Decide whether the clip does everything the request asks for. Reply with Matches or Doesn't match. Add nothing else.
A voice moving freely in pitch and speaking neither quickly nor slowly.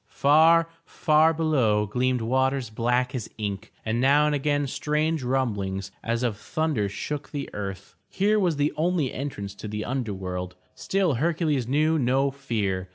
Matches